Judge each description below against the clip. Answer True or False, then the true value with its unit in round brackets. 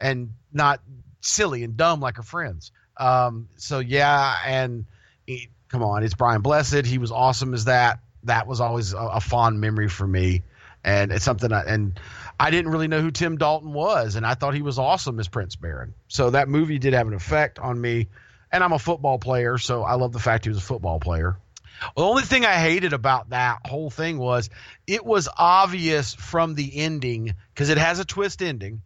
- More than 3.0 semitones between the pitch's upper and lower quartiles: True (4.8 semitones)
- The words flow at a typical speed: False (210 wpm)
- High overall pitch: False (125 Hz)